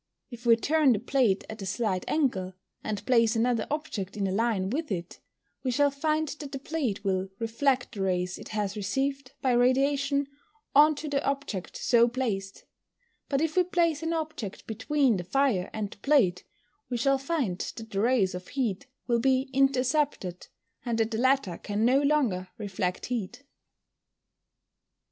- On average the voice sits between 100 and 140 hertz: No, high, 245 Hz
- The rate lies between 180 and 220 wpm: No, average, 170 wpm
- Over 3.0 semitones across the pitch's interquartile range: Yes, wide, 5.6 semitones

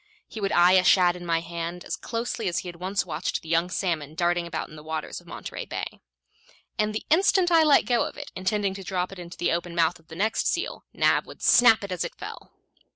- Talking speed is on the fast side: Yes, fast, 245 wpm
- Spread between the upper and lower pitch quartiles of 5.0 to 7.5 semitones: No, average, 3.4 semitones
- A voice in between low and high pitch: Yes, medium, 180 Hz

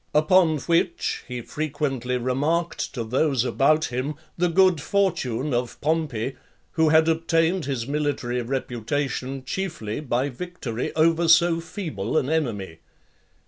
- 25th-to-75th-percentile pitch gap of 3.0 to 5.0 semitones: Yes, average, 4.7 semitones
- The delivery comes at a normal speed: No, slow, 125 wpm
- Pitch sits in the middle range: Yes, medium, 150 Hz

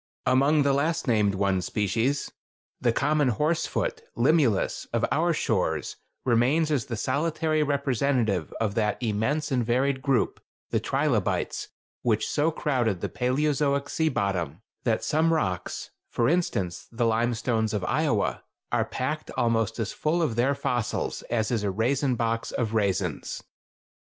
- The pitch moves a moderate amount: Yes, average, 4.6 semitones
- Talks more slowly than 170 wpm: Yes, average, 140 wpm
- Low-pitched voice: Yes, low, 120 Hz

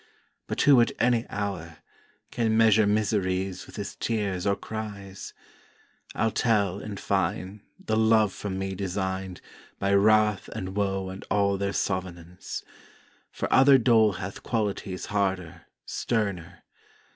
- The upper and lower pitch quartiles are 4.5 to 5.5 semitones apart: No, narrow, 2.4 semitones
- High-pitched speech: No, low, 100 Hz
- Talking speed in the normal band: No, slow, 130 wpm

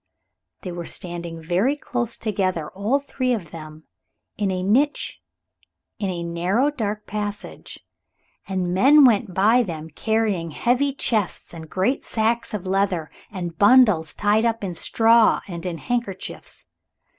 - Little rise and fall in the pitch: No, average, 4.9 semitones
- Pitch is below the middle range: No, high, 200 Hz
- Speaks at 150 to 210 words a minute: No, average, 140 wpm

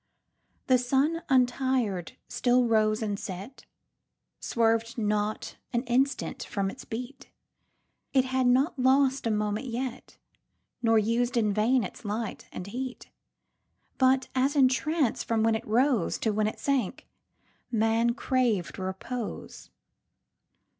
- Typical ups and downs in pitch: Yes, average, 3.3 semitones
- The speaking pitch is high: Yes, high, 240 Hz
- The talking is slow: Yes, slow, 115 wpm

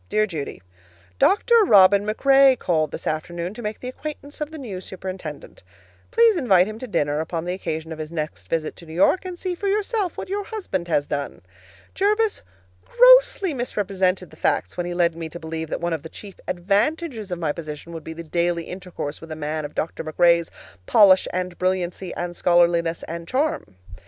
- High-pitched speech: No, medium, 180 Hz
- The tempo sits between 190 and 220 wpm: Yes, average, 195 wpm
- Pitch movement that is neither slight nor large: No, wide, 7.7 semitones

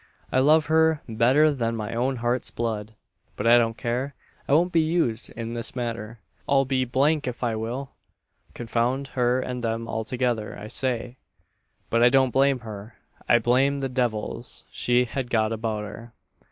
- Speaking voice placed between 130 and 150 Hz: No, low, 120 Hz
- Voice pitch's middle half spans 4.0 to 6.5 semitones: No, narrow, 2.6 semitones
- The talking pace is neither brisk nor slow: Yes, average, 175 wpm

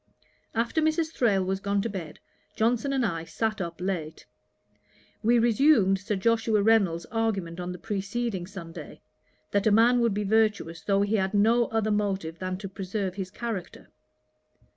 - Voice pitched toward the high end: Yes, high, 205 Hz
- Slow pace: No, average, 165 wpm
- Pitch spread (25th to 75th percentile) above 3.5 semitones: No, average, 3.2 semitones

